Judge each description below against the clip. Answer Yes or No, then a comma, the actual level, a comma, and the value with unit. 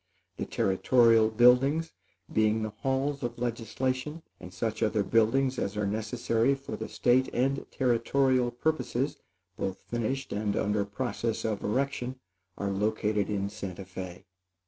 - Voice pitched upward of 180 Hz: No, low, 115 Hz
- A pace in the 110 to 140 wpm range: Yes, slow, 135 wpm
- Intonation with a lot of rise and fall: No, average, 3.8 semitones